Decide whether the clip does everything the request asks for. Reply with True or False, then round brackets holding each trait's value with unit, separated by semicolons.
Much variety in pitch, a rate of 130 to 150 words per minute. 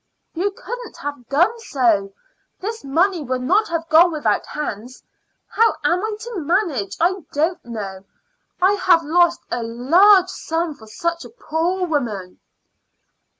True (6.8 semitones; 145 wpm)